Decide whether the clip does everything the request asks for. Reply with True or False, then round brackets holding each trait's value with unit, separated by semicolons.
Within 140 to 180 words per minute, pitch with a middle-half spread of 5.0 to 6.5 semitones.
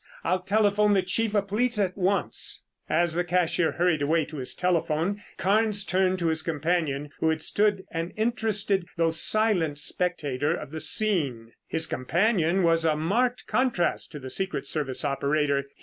False (165 wpm; 4.5 semitones)